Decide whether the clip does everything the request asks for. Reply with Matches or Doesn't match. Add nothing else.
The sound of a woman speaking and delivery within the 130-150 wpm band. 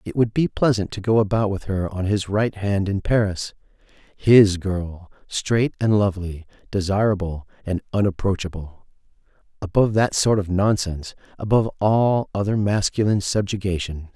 Doesn't match